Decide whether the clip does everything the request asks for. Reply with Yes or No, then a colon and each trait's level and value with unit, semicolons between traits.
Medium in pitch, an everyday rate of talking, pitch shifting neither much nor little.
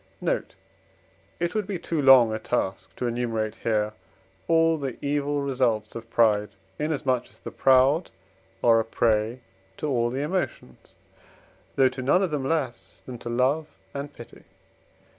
No: low, 130 Hz; average, 155 wpm; average, 4.1 semitones